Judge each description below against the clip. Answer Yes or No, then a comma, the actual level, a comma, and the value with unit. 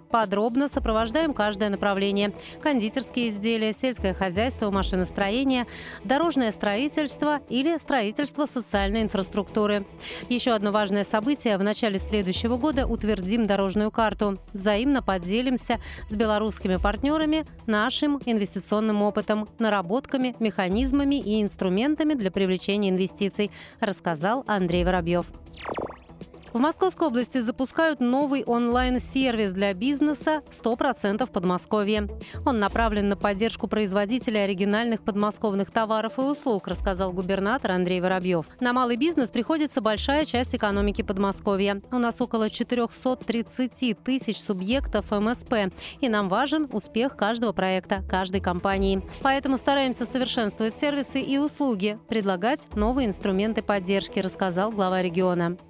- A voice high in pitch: Yes, high, 220 Hz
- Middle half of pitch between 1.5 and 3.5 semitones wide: No, average, 4.2 semitones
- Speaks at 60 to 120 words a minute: Yes, slow, 110 wpm